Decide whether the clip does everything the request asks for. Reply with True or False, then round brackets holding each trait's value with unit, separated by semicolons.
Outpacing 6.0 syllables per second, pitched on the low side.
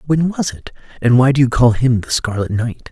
False (5.2 syllables/s; 125 Hz)